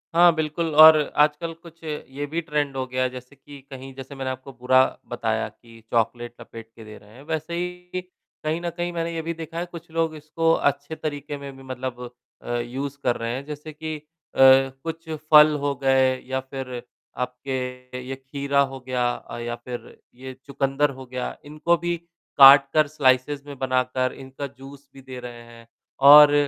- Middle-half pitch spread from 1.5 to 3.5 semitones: Yes, average, 3.1 semitones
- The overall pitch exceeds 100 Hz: Yes, low, 135 Hz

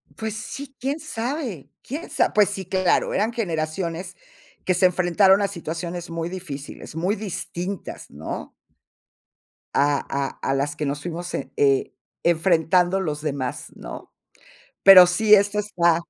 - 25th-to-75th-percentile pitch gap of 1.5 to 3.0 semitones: No, average, 4.0 semitones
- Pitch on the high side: No, medium, 180 Hz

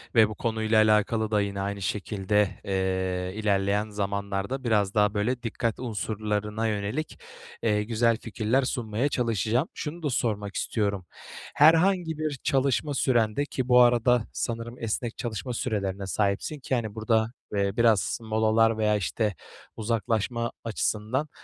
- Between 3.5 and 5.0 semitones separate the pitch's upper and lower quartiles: No, average, 2.8 semitones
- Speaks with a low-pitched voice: Yes, low, 110 Hz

